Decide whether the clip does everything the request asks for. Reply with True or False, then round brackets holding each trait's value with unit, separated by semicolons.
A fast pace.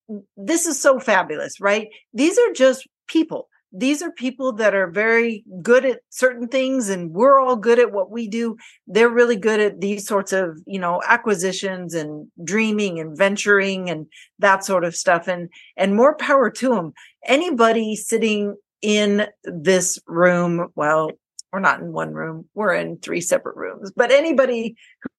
False (170 wpm)